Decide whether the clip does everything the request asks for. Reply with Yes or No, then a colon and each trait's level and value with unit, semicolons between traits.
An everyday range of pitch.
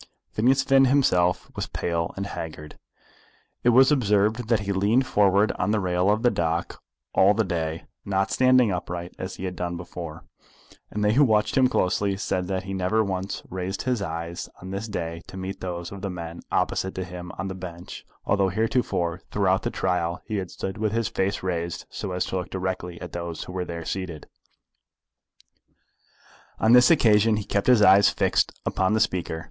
Yes: average, 3.2 semitones